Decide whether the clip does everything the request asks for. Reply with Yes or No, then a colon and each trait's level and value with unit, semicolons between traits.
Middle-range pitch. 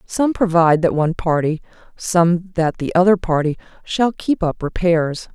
Yes: medium, 175 Hz